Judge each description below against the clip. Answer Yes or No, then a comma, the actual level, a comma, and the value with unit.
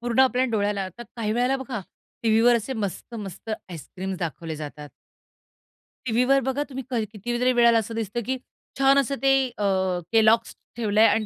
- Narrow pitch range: No, average, 3.4 semitones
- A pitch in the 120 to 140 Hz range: No, high, 230 Hz